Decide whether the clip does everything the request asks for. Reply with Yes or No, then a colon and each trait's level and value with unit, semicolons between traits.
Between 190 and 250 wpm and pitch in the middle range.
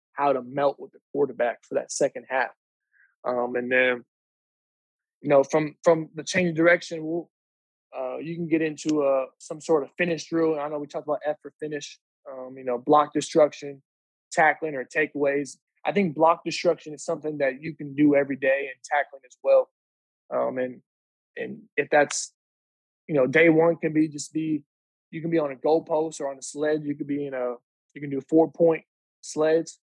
Yes: average, 200 wpm; medium, 150 Hz